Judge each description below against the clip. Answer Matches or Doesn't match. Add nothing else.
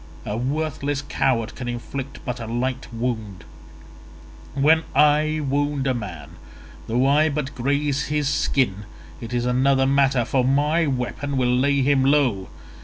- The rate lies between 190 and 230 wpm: Doesn't match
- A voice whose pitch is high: Doesn't match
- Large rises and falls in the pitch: Doesn't match